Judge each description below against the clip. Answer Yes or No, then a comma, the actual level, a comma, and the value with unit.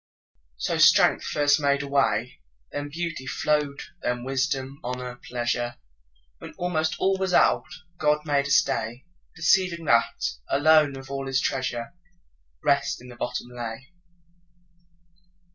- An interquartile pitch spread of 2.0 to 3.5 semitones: No, average, 3.9 semitones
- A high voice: No, low, 135 Hz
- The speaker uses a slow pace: Yes, slow, 115 wpm